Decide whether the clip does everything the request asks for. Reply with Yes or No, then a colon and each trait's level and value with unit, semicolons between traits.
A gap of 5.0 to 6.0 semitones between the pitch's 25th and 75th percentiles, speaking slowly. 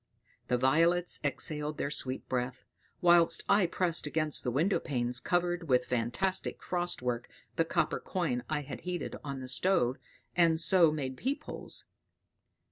No: average, 5.3 semitones; average, 145 wpm